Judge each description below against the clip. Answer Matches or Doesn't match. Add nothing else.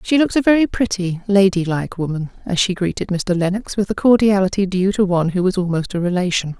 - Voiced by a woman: Matches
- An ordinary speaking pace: Doesn't match